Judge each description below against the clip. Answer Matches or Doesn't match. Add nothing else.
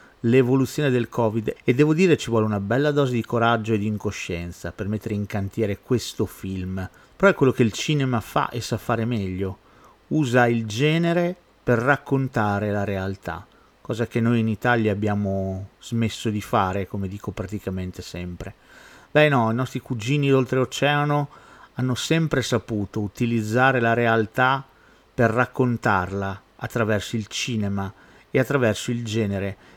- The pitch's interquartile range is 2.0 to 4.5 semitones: Matches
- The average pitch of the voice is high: Doesn't match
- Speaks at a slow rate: Doesn't match